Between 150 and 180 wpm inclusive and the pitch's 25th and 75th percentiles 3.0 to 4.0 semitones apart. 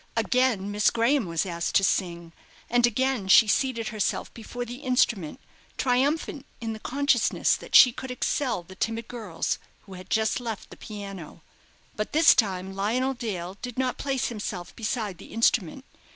No: average, 165 wpm; average, 4.5 semitones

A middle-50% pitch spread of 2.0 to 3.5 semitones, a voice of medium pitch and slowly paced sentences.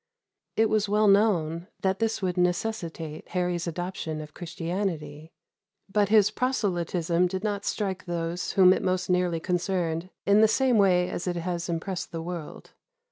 No: average, 3.0 semitones; medium, 180 Hz; average, 155 wpm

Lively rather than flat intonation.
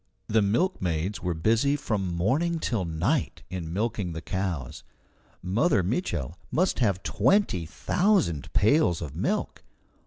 Yes: wide, 7.9 semitones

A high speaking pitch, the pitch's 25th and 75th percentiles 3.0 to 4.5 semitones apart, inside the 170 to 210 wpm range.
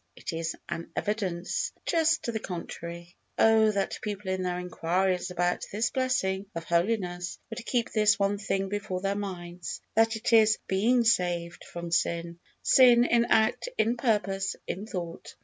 No: high, 195 Hz; average, 4.0 semitones; average, 160 wpm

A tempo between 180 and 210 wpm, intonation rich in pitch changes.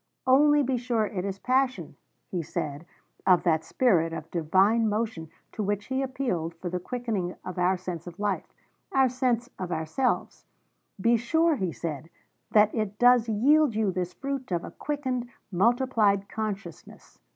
No: average, 160 wpm; wide, 5.8 semitones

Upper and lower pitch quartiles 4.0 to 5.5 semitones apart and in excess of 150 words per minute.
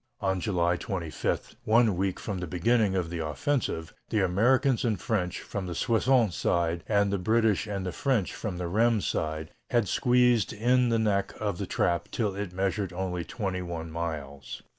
Yes: average, 4.3 semitones; average, 175 wpm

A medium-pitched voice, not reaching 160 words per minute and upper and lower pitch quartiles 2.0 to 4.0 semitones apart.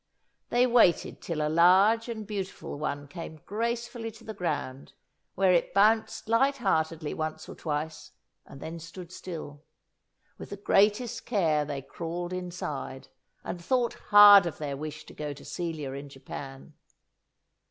No: medium, 170 Hz; average, 150 wpm; wide, 5.4 semitones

